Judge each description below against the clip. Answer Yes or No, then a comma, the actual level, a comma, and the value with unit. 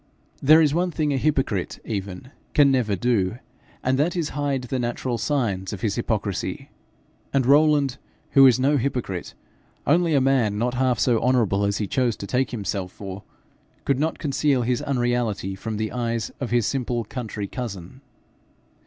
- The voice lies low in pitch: Yes, low, 125 Hz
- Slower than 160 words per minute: No, average, 170 wpm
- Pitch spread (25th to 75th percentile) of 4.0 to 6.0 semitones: Yes, average, 4.5 semitones